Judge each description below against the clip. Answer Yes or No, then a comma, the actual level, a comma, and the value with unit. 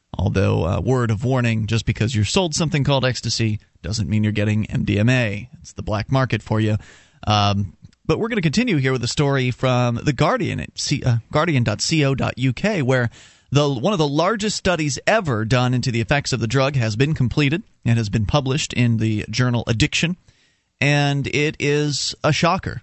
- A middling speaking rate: Yes, average, 185 wpm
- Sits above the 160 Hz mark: No, low, 125 Hz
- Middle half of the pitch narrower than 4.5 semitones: No, average, 5.0 semitones